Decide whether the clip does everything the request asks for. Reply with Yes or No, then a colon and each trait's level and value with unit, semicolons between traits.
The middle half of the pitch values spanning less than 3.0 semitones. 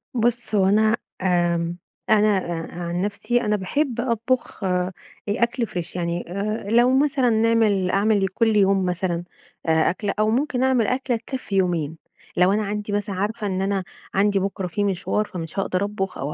No: average, 3.6 semitones